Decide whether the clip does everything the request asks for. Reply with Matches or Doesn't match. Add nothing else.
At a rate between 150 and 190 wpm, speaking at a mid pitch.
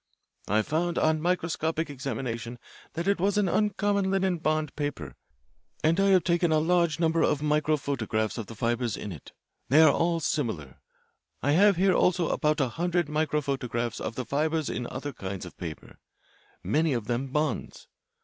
Matches